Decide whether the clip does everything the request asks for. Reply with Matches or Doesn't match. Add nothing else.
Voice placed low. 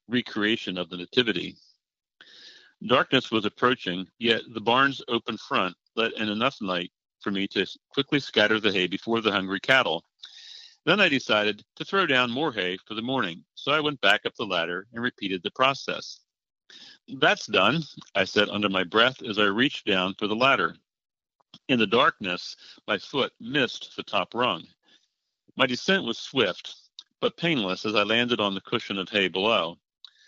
Matches